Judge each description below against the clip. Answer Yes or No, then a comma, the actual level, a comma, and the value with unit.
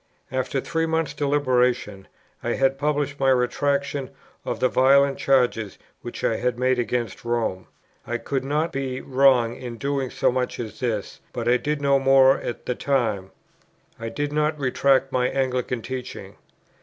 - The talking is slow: No, average, 160 wpm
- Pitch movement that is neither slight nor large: No, narrow, 2.3 semitones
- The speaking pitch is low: Yes, low, 130 Hz